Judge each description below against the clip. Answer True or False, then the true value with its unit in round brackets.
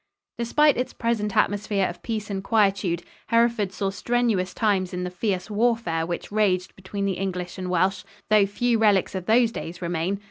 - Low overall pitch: False (200 Hz)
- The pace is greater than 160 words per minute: True (175 wpm)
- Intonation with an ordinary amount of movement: True (3.4 semitones)